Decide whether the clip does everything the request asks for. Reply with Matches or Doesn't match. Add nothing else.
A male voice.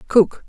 Matches